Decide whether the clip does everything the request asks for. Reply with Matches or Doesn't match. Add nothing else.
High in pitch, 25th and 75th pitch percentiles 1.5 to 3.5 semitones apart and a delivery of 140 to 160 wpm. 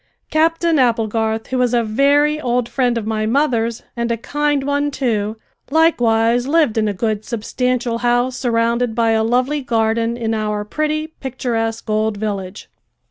Matches